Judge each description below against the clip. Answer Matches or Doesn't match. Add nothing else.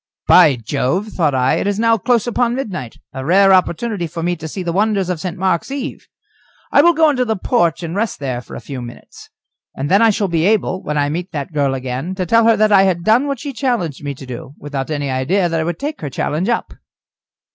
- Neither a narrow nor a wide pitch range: Doesn't match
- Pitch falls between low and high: Matches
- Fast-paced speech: Matches